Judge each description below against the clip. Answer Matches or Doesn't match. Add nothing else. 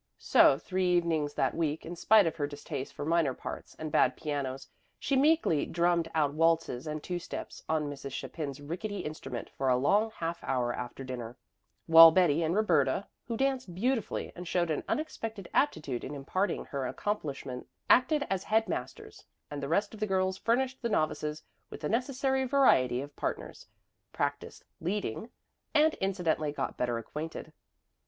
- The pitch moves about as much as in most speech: Doesn't match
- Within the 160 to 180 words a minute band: Matches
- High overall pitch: Doesn't match